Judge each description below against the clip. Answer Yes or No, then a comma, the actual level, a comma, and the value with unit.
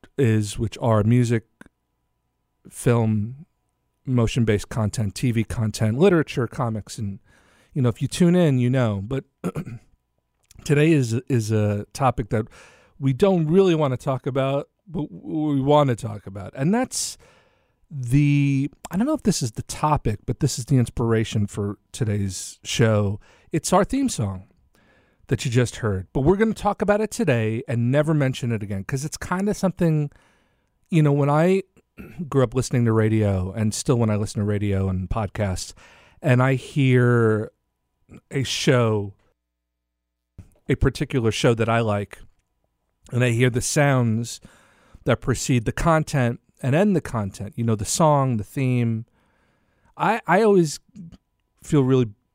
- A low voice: Yes, low, 125 Hz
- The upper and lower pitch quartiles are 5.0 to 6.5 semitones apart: Yes, average, 5.3 semitones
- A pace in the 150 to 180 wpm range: Yes, average, 160 wpm